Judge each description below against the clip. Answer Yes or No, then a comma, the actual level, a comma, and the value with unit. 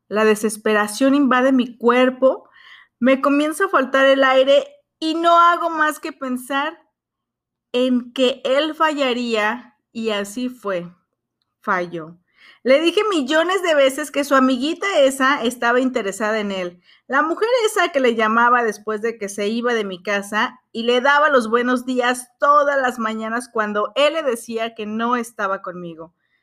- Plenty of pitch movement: No, average, 4.5 semitones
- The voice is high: Yes, very high, 250 Hz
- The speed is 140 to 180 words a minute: Yes, average, 155 wpm